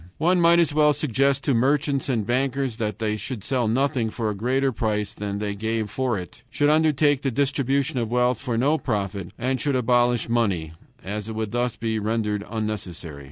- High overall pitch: No, low, 120 Hz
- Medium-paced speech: Yes, average, 195 wpm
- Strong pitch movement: No, average, 4.3 semitones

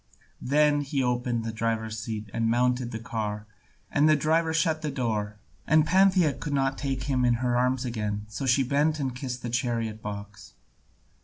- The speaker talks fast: No, average, 180 wpm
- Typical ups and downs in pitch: Yes, average, 4.1 semitones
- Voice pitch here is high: No, low, 125 Hz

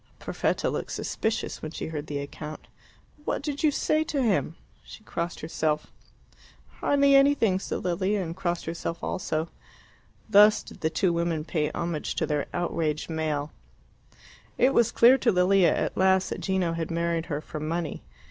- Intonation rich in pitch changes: No, average, 4.5 semitones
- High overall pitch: No, medium, 170 Hz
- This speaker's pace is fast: No, average, 165 wpm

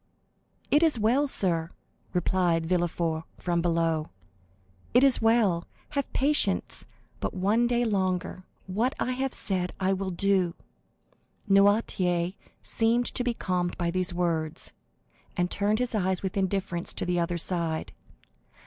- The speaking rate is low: Yes, slow, 130 wpm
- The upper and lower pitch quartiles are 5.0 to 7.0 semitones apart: No, average, 4.4 semitones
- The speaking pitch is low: No, medium, 185 Hz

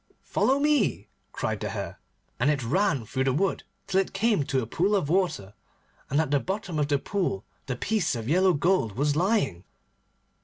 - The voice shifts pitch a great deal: Yes, wide, 6.6 semitones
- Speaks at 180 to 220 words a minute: Yes, average, 190 wpm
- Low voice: No, medium, 155 Hz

